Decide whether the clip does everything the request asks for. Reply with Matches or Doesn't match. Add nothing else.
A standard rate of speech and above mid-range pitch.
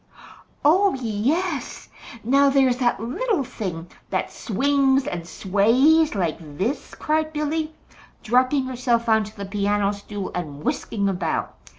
Doesn't match